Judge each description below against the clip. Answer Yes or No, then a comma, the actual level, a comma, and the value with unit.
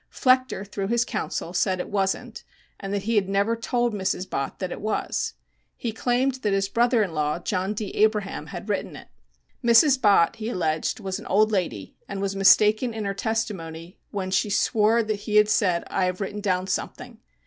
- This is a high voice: Yes, high, 205 Hz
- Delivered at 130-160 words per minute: No, average, 195 wpm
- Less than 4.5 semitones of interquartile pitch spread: Yes, average, 2.9 semitones